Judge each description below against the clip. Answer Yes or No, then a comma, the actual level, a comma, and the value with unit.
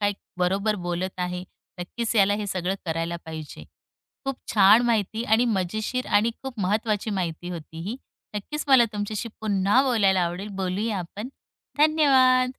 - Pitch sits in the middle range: No, high, 205 Hz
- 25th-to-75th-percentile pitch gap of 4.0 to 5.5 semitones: Yes, average, 4.3 semitones